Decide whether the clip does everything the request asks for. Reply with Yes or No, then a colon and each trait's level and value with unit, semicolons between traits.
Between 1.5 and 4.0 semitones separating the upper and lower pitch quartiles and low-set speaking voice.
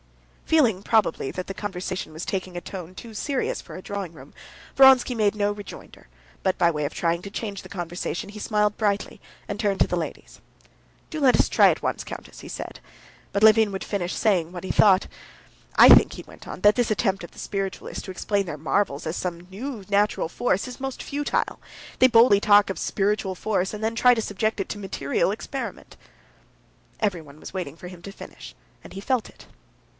No: average, 3.0 semitones; high, 200 Hz